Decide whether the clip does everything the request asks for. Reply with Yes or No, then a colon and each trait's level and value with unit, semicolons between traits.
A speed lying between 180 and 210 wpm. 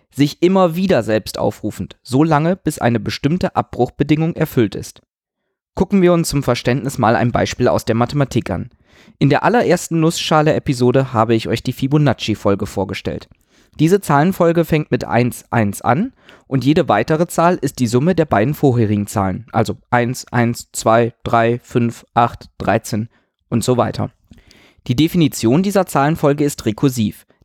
No: average, 150 wpm